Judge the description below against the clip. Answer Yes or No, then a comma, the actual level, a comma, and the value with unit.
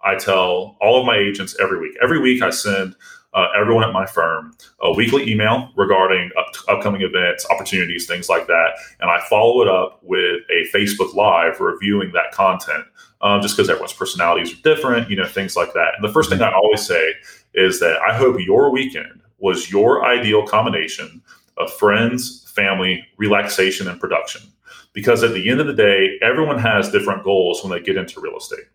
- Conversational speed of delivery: Yes, average, 190 wpm